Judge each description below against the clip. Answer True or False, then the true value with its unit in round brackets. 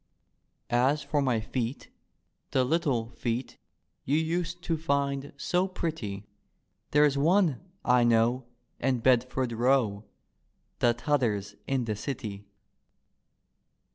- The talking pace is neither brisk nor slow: False (110 wpm)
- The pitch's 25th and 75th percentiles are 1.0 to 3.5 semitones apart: False (4.1 semitones)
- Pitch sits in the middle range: False (130 Hz)